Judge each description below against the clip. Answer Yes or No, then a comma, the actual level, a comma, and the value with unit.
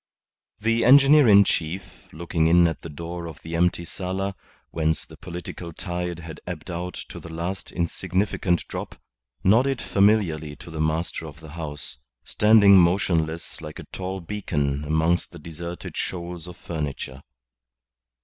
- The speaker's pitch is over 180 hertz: No, very low, 85 Hz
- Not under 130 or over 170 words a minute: Yes, average, 150 wpm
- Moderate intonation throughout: Yes, average, 3.0 semitones